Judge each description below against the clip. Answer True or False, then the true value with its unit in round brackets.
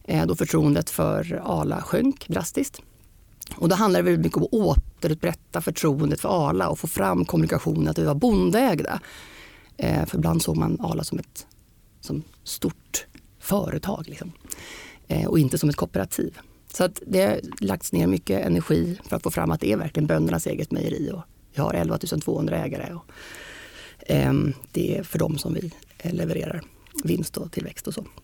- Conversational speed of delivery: True (170 wpm)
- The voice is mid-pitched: True (160 Hz)